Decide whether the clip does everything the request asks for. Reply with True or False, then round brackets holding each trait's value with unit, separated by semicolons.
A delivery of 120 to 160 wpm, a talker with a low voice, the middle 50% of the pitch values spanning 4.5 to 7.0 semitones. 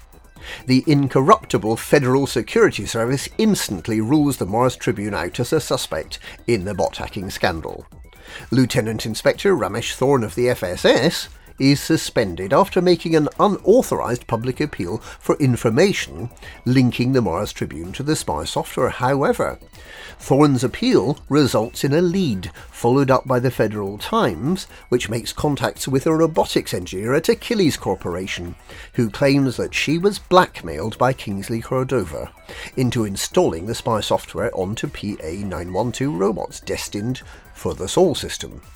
True (140 wpm; 125 Hz; 4.8 semitones)